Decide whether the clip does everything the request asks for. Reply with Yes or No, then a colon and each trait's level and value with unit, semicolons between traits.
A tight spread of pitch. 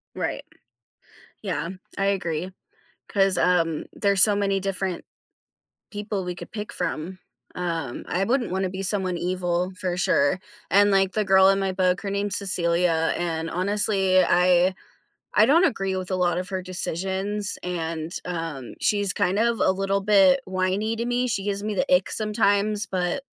Yes: narrow, 2.2 semitones